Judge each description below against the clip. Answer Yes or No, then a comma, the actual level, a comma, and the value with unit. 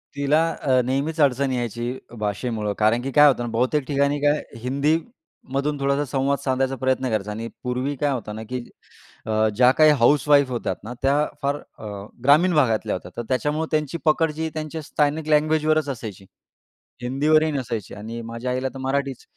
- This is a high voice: No, low, 135 Hz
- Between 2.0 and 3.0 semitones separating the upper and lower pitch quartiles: No, average, 3.5 semitones